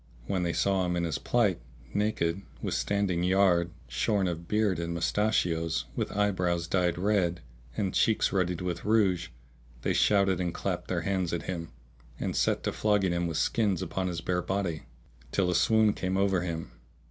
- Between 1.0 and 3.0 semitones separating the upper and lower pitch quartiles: Yes, narrow, 2.6 semitones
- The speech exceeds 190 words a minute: No, average, 175 wpm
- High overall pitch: No, very low, 90 Hz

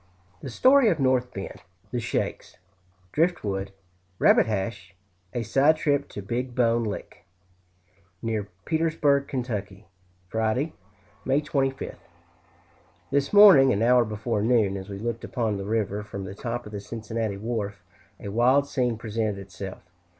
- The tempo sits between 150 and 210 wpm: No, average, 140 wpm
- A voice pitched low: Yes, low, 115 Hz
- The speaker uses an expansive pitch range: No, average, 4.6 semitones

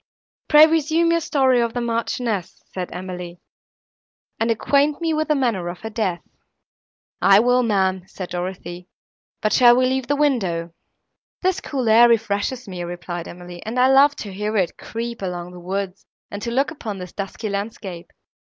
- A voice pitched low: No, high, 220 Hz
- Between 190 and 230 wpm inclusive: No, average, 170 wpm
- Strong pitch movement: Yes, wide, 5.9 semitones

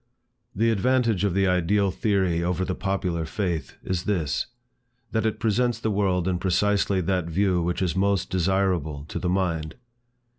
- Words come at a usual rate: Yes, average, 160 wpm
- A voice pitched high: No, very low, 95 Hz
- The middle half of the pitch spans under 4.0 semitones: Yes, narrow, 2.5 semitones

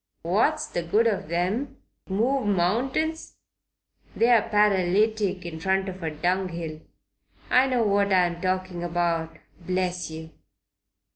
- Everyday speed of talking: No, slow, 120 wpm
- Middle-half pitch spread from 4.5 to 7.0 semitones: No, average, 3.9 semitones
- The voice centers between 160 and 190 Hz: Yes, medium, 185 Hz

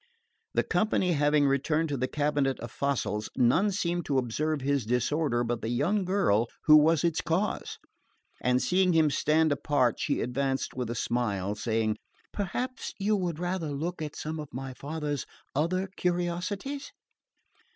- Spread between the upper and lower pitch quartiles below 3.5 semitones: No, wide, 5.5 semitones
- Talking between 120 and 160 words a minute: Yes, average, 155 wpm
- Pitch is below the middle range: No, medium, 150 Hz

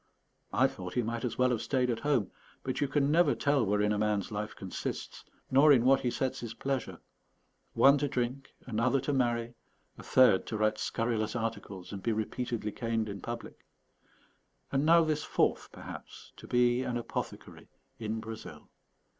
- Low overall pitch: Yes, low, 120 Hz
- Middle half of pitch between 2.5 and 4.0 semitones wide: Yes, average, 3.5 semitones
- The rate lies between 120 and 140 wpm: No, average, 175 wpm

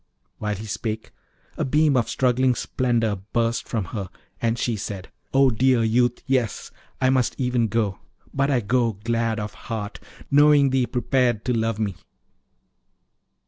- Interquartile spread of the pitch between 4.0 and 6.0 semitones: No, average, 2.7 semitones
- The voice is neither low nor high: No, low, 115 Hz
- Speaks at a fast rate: No, average, 155 wpm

